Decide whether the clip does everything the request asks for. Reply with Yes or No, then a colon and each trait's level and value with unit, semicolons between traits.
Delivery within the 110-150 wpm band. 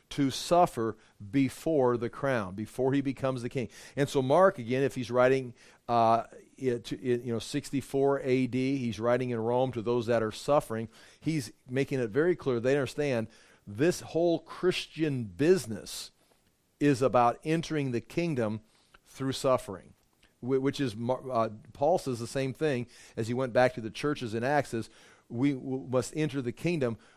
No: average, 165 wpm